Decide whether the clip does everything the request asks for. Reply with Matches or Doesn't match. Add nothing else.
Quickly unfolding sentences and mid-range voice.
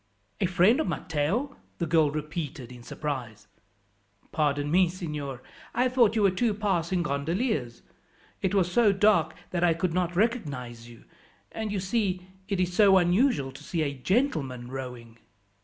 Doesn't match